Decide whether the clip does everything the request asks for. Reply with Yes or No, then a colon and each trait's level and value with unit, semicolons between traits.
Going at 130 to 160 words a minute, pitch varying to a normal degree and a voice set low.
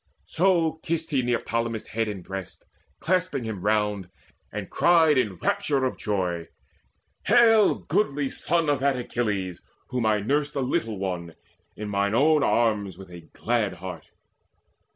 No: average, 145 wpm; wide, 6.8 semitones; low, 115 Hz